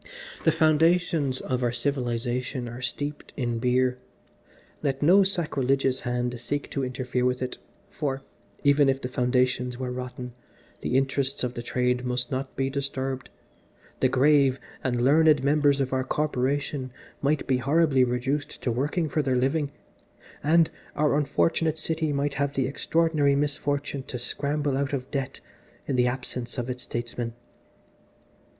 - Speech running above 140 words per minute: Yes, average, 150 wpm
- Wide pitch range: No, narrow, 2.4 semitones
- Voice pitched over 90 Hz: Yes, low, 135 Hz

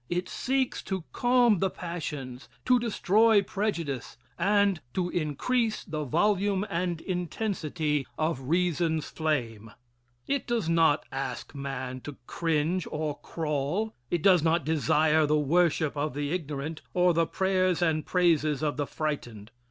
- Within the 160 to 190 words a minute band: No, slow, 135 wpm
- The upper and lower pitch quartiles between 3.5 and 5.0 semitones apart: Yes, average, 4.0 semitones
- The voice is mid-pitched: Yes, medium, 165 Hz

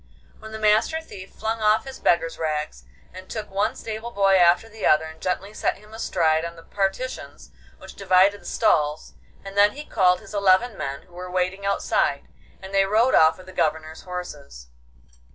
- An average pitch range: Yes, average, 4.0 semitones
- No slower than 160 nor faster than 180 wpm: No, average, 190 wpm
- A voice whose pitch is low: No, high, 190 Hz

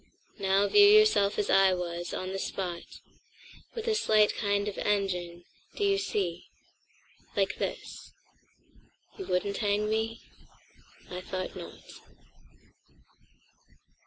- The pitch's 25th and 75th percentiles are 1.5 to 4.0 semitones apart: Yes, average, 3.0 semitones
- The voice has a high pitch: Yes, high, 200 Hz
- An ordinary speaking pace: No, slow, 105 wpm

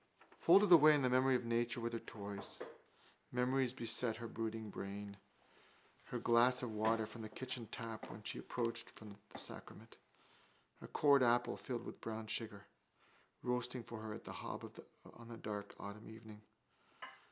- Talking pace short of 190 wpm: Yes, average, 165 wpm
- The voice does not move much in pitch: Yes, narrow, 2.3 semitones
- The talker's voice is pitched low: Yes, low, 115 Hz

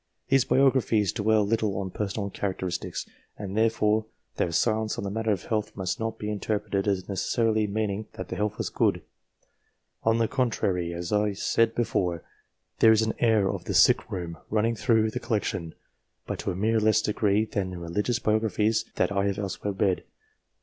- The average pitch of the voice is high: No, low, 105 Hz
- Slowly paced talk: No, average, 185 wpm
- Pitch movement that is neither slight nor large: No, narrow, 2.2 semitones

